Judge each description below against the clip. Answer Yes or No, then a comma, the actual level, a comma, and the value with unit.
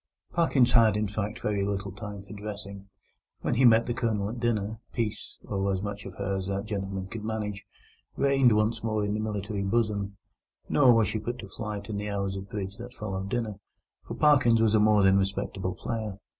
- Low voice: Yes, low, 105 Hz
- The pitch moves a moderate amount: No, narrow, 2.3 semitones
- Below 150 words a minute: No, average, 200 wpm